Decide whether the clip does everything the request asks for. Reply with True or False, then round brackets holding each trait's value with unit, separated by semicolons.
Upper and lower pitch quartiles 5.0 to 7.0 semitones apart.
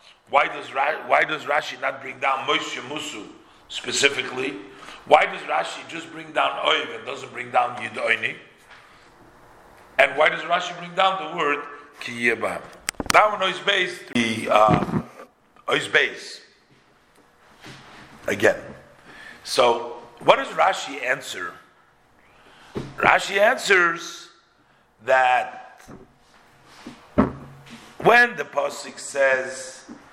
True (5.3 semitones)